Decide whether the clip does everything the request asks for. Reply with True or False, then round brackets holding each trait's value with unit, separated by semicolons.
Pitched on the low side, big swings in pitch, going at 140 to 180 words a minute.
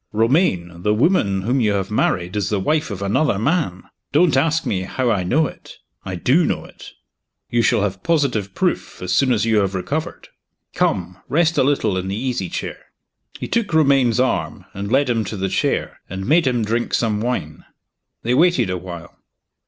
False (110 Hz; 6.5 semitones; 190 wpm)